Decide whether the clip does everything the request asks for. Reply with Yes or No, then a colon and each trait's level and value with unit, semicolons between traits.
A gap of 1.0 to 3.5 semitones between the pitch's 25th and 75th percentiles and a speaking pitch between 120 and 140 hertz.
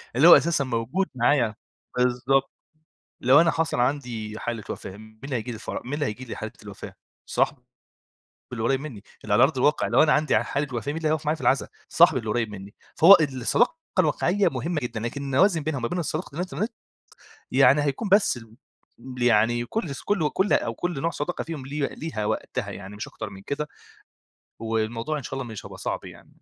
No: average, 5.1 semitones; low, 135 Hz